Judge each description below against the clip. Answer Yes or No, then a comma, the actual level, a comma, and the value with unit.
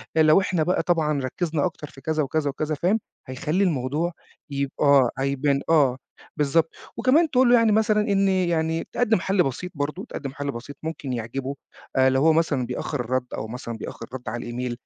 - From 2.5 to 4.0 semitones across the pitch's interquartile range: No, average, 4.8 semitones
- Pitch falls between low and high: Yes, medium, 150 Hz